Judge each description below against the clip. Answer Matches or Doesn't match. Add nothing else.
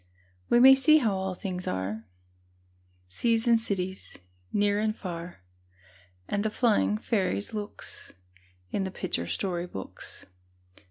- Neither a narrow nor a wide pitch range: Matches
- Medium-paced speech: Doesn't match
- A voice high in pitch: Matches